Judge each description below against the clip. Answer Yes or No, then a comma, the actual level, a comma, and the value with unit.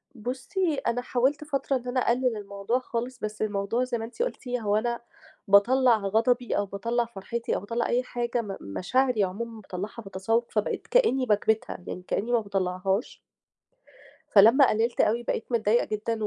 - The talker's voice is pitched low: No, high, 230 Hz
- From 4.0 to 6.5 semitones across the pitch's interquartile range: No, average, 3.2 semitones